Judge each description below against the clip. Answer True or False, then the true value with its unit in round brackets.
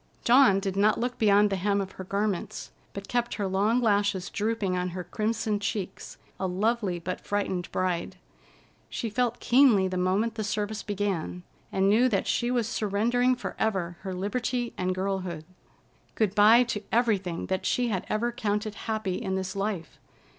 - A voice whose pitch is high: True (205 Hz)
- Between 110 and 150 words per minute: False (170 wpm)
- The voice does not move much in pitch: False (3.1 semitones)